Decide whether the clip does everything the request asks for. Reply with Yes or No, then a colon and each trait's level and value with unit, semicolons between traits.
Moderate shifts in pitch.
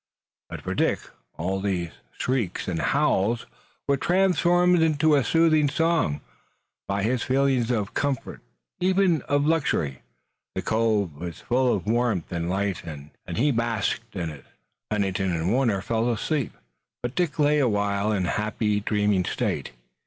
No: wide, 6.8 semitones